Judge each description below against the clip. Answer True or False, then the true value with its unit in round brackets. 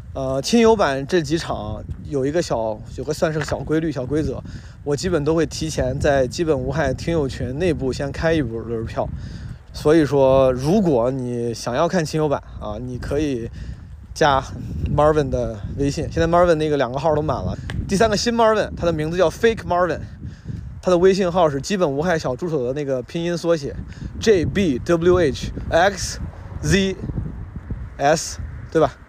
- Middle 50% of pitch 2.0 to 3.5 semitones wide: False (5.2 semitones)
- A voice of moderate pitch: True (145 Hz)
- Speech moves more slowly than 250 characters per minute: False (295 characters per minute)